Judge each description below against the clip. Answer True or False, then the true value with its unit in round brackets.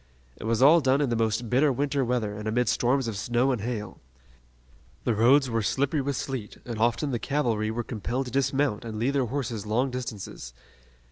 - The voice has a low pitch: True (120 Hz)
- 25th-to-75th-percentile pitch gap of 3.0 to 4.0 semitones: True (3.3 semitones)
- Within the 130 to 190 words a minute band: False (200 wpm)